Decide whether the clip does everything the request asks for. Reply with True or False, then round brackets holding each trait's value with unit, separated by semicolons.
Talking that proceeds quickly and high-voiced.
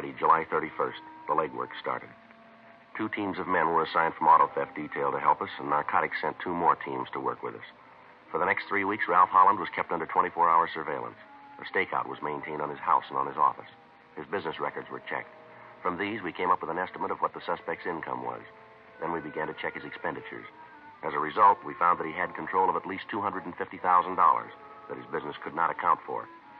True (220 wpm; 295 Hz)